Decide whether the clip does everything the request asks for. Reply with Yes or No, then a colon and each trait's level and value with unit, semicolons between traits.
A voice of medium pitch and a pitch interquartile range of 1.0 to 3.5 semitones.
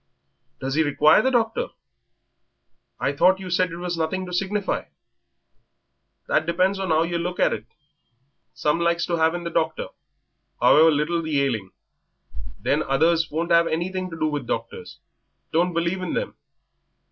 Yes: medium, 170 Hz; narrow, 2.5 semitones